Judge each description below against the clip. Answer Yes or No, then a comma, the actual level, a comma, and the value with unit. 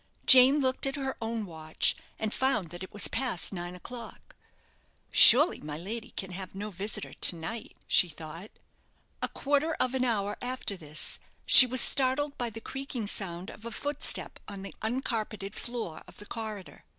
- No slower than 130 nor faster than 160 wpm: No, average, 175 wpm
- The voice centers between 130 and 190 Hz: No, high, 220 Hz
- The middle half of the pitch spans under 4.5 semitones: No, average, 5.2 semitones